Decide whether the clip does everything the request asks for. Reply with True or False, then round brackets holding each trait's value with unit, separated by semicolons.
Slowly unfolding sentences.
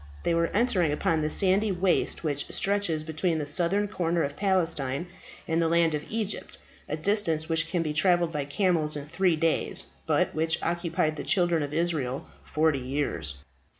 False (175 wpm)